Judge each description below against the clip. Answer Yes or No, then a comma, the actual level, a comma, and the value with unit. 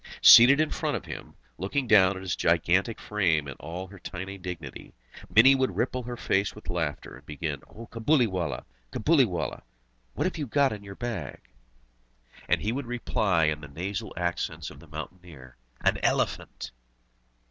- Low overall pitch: Yes, very low, 95 Hz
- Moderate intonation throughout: No, wide, 5.9 semitones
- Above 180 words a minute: No, average, 165 wpm